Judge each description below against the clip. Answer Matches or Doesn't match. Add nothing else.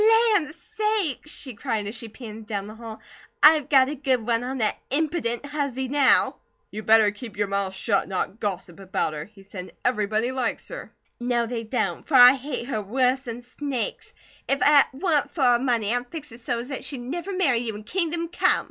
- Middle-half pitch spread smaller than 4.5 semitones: Doesn't match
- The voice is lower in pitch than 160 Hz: Doesn't match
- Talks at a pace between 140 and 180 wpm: Doesn't match